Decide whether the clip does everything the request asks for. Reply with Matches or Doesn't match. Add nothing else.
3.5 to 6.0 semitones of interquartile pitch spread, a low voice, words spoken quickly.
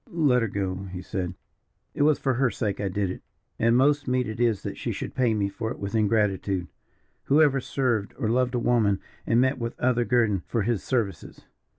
Matches